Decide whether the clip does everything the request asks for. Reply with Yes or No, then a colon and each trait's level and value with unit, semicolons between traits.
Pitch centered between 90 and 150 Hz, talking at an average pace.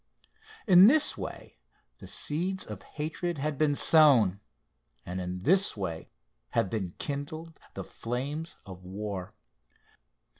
No: medium, 140 Hz; slow, 120 wpm